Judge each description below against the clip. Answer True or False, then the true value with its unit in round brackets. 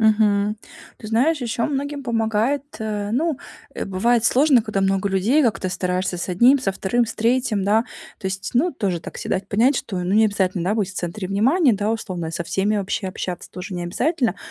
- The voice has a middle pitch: False (210 Hz)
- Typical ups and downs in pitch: True (4.1 semitones)